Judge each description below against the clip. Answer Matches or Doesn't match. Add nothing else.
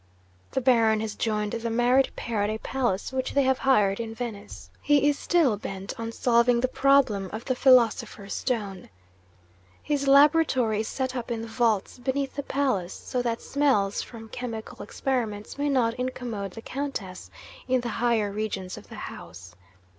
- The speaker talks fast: Doesn't match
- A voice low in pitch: Doesn't match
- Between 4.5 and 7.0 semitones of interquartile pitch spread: Doesn't match